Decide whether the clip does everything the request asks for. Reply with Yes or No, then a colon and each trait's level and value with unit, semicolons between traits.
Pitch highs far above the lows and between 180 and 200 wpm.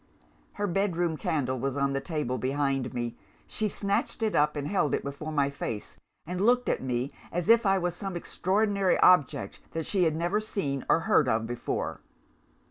Yes: wide, 6.0 semitones; average, 185 wpm